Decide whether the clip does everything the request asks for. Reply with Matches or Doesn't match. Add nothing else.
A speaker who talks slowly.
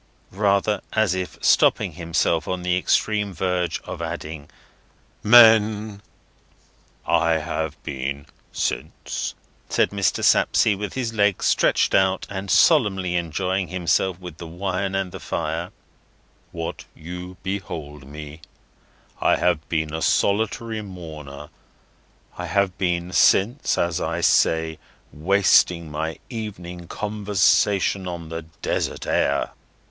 Matches